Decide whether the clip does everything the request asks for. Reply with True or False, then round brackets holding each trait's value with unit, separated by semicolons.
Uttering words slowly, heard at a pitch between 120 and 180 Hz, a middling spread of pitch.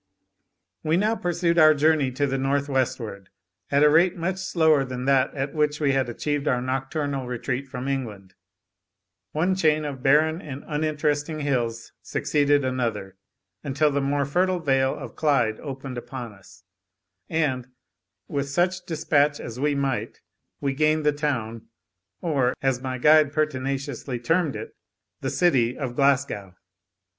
False (150 wpm; 140 Hz; 3.0 semitones)